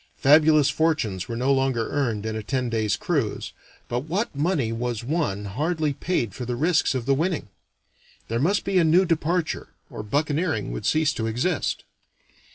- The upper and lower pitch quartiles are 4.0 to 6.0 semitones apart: Yes, wide, 5.5 semitones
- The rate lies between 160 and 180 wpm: Yes, average, 170 wpm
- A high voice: No, medium, 140 Hz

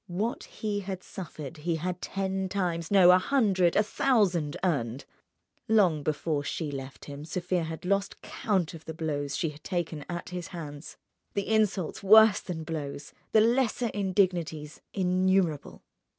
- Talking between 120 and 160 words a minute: Yes, average, 145 wpm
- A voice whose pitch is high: No, medium, 180 Hz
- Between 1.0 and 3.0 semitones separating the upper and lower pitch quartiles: No, average, 4.0 semitones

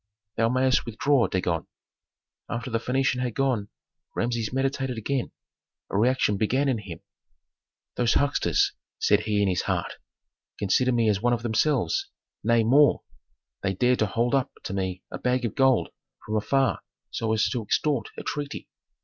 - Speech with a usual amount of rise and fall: Yes, average, 3.6 semitones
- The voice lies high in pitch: No, low, 120 Hz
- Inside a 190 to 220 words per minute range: No, average, 160 wpm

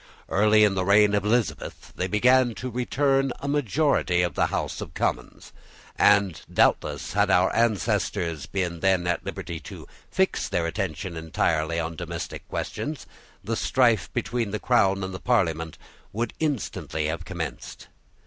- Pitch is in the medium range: No, low, 100 Hz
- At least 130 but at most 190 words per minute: Yes, average, 150 wpm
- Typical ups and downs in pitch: No, wide, 5.8 semitones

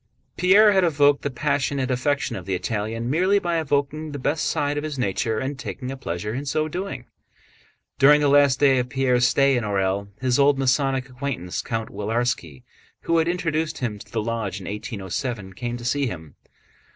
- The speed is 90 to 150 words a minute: No, average, 190 wpm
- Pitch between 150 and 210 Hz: No, low, 130 Hz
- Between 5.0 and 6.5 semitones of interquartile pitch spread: No, average, 4.4 semitones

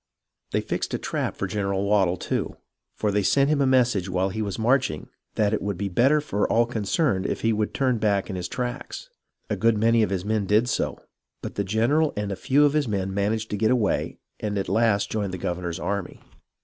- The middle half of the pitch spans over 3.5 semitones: No, average, 3.2 semitones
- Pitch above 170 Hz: No, low, 105 Hz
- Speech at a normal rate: No, fast, 225 wpm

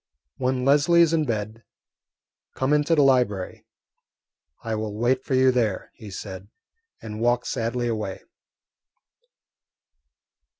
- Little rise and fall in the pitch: No, average, 3.5 semitones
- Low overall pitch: Yes, low, 120 Hz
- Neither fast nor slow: No, slow, 120 wpm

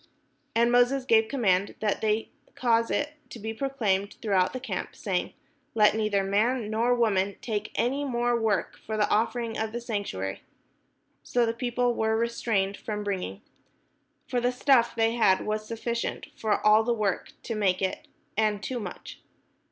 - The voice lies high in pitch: Yes, high, 220 Hz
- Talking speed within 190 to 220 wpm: No, average, 165 wpm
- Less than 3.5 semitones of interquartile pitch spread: Yes, narrow, 2.6 semitones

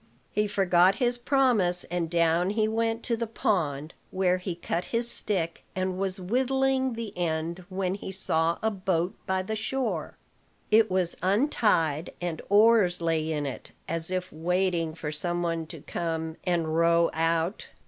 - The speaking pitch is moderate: Yes, medium, 180 Hz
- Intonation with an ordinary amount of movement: Yes, average, 4.2 semitones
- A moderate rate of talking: Yes, average, 160 wpm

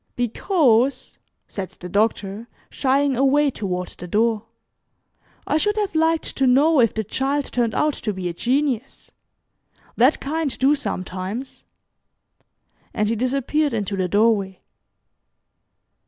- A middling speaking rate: No, slow, 125 wpm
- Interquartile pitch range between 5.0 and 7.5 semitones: Yes, wide, 5.4 semitones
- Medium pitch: No, high, 245 Hz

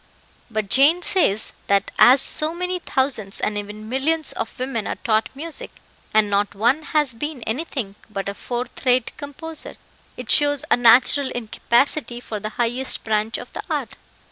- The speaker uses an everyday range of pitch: Yes, average, 5.0 semitones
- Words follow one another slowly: No, average, 165 wpm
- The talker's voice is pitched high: Yes, high, 245 Hz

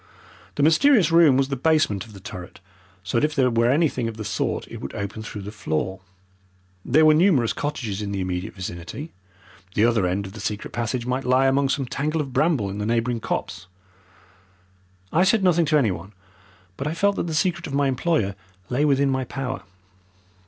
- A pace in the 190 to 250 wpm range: Yes, average, 200 wpm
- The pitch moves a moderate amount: No, wide, 6.5 semitones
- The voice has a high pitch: No, low, 125 Hz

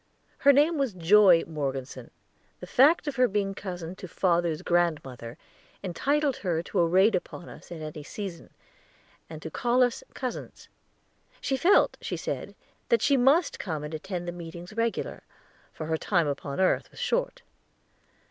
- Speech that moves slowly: No, average, 160 wpm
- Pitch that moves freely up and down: Yes, wide, 7.1 semitones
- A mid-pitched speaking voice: Yes, medium, 180 Hz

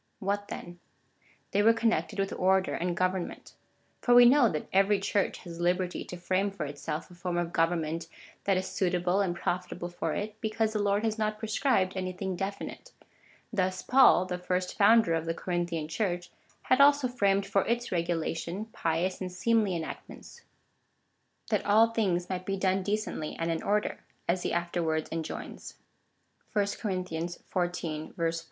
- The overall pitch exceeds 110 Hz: Yes, medium, 185 Hz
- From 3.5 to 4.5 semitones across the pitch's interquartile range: No, average, 3.0 semitones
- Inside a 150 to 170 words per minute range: Yes, average, 165 wpm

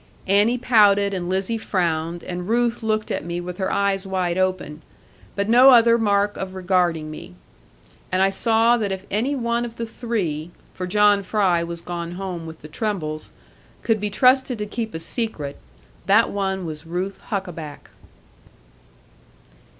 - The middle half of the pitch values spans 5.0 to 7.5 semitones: No, average, 4.1 semitones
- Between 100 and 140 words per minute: No, average, 160 wpm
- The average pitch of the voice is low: No, high, 195 Hz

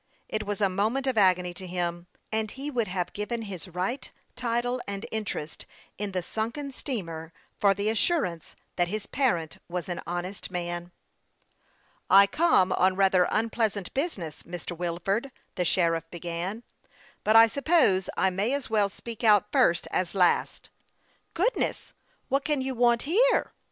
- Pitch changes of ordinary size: Yes, average, 4.9 semitones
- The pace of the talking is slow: No, average, 165 wpm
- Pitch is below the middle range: No, high, 200 Hz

